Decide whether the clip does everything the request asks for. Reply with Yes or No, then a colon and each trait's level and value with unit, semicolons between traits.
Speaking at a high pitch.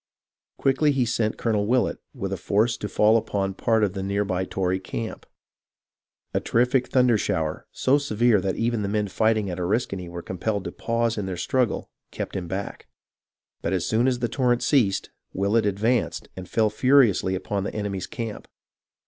No: low, 105 Hz